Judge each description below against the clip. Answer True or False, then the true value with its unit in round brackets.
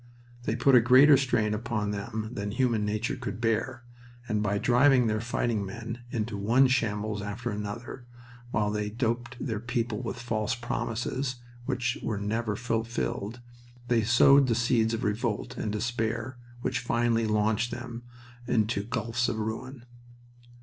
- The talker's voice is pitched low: True (115 Hz)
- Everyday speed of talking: True (150 wpm)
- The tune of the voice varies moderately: False (2.2 semitones)